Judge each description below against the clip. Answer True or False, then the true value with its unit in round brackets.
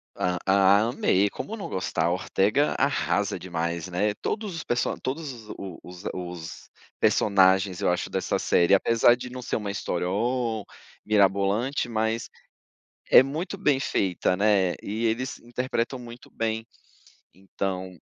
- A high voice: False (105 Hz)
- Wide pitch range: False (4.6 semitones)